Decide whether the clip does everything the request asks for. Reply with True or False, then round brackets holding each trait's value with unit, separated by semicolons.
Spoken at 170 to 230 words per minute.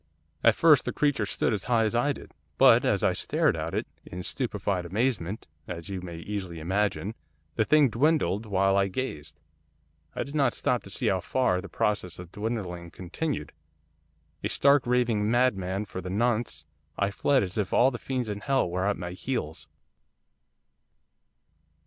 True (175 wpm)